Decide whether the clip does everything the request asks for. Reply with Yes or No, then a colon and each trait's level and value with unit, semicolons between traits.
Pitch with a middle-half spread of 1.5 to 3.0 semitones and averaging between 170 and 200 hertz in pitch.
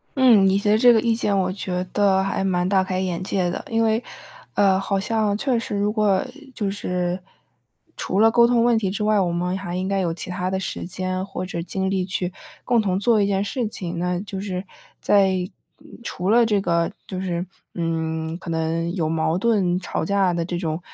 Yes: narrow, 2.5 semitones; high, 190 Hz